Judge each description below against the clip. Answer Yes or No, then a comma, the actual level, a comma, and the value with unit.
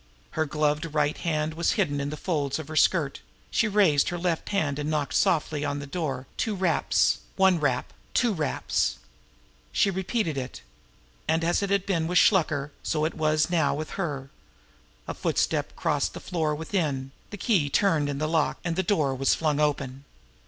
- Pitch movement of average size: Yes, average, 3.5 semitones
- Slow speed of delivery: No, average, 185 wpm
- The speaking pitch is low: No, medium, 155 Hz